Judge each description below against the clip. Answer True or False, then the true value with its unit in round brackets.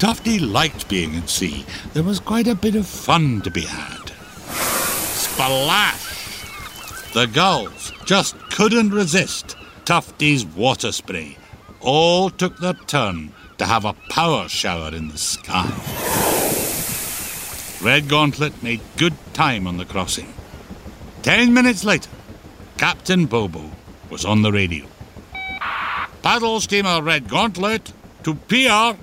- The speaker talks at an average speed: False (120 wpm)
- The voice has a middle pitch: True (145 Hz)